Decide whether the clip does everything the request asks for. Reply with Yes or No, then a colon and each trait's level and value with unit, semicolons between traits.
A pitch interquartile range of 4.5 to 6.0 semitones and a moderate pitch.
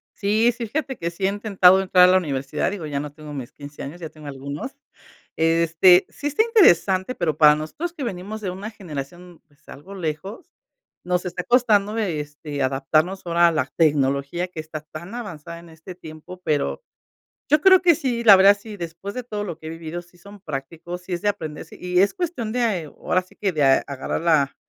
Yes: average, 4.8 semitones; medium, 175 Hz